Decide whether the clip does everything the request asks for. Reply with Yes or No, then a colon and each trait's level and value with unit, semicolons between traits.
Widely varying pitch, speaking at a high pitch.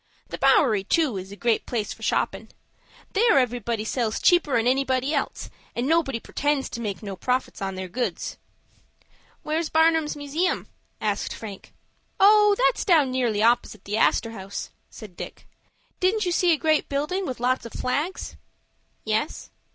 Yes: wide, 6.2 semitones; very high, 255 Hz